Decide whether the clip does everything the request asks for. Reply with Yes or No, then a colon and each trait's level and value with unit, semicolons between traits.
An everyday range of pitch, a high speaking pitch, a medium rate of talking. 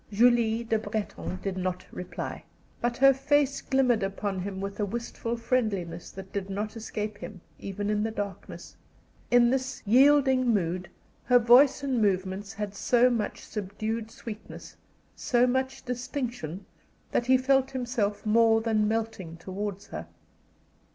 Yes: average, 3.7 semitones; high, 220 Hz; average, 145 wpm